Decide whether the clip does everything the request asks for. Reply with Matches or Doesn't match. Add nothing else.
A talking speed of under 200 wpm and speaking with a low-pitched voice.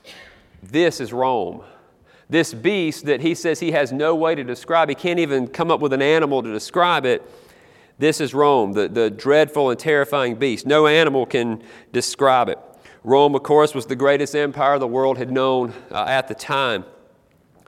Doesn't match